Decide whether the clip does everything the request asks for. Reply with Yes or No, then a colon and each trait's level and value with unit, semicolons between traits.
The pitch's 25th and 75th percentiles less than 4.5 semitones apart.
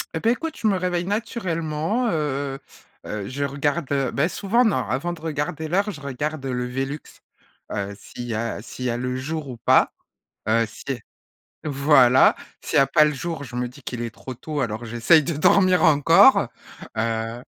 No: average, 4.9 semitones